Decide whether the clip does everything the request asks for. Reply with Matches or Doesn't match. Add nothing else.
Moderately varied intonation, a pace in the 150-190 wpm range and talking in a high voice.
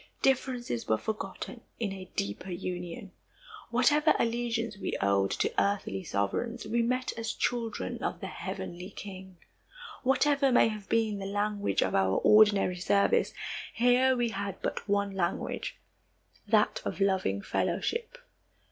Doesn't match